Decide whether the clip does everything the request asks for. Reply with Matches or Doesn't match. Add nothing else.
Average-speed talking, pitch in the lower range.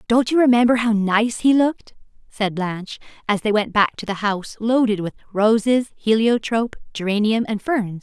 Doesn't match